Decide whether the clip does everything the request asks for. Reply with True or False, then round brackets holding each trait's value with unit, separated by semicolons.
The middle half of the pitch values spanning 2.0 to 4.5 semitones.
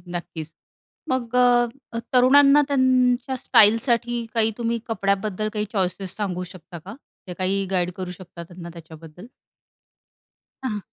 False (5.0 semitones)